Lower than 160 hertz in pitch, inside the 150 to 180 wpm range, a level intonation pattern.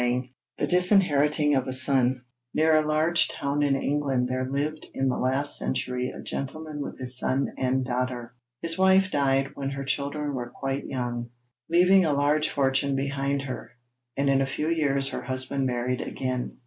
Yes: medium, 140 Hz; average, 175 wpm; narrow, 2.3 semitones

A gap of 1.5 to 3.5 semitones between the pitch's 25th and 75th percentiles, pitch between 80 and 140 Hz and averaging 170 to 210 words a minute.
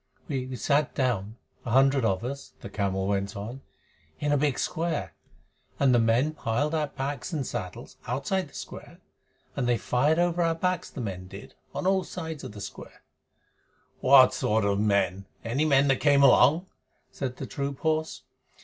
No: wide, 5.5 semitones; low, 135 Hz; average, 175 wpm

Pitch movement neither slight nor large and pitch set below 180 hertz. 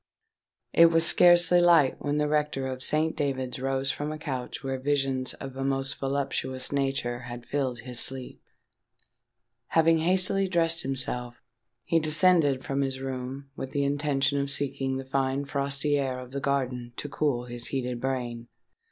No: narrow, 2.2 semitones; low, 135 Hz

